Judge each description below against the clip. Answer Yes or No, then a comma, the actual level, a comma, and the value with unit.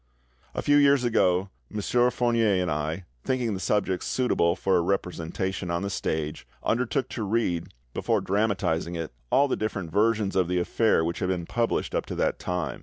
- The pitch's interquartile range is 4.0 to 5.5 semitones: Yes, average, 4.8 semitones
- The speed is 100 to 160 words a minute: No, average, 180 wpm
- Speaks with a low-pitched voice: Yes, very low, 95 Hz